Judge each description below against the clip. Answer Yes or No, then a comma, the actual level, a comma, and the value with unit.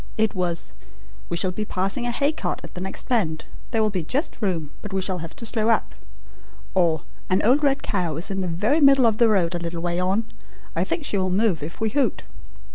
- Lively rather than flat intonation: No, average, 4.7 semitones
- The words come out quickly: Yes, fast, 235 wpm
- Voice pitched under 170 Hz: No, high, 195 Hz